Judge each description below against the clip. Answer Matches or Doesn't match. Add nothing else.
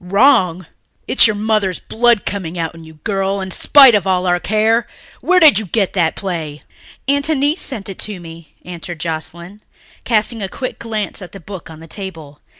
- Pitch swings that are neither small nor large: Matches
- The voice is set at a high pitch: Matches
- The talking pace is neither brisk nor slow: Matches